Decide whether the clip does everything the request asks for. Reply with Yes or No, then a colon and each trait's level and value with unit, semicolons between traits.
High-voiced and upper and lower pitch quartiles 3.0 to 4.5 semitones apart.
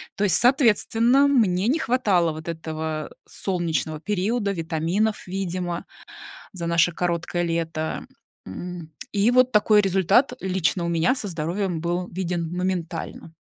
No: medium, 180 Hz; average, 3.8 semitones